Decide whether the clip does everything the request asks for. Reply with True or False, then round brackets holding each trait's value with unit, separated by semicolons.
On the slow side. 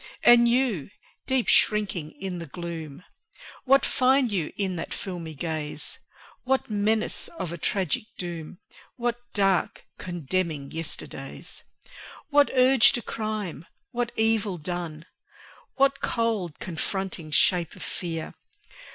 True (115 wpm)